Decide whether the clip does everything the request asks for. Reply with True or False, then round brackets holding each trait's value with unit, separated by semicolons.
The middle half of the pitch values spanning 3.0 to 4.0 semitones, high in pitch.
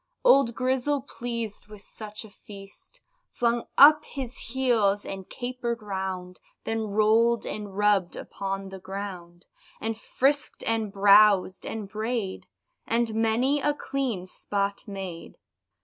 True (3.4 semitones; 215 Hz)